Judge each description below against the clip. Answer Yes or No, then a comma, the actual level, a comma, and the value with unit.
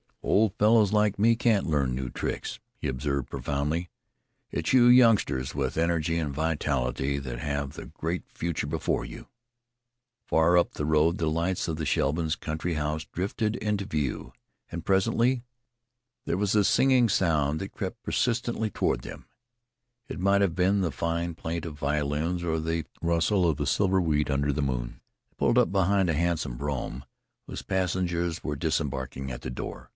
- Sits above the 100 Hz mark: No, very low, 80 Hz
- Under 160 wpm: No, average, 170 wpm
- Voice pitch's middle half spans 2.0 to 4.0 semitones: No, average, 4.7 semitones